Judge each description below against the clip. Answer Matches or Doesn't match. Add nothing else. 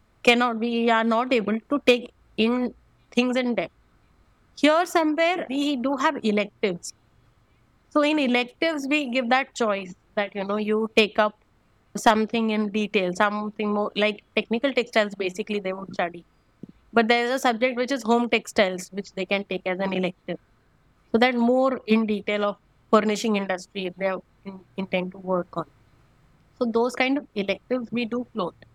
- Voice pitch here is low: Doesn't match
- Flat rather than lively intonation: Doesn't match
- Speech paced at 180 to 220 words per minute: Doesn't match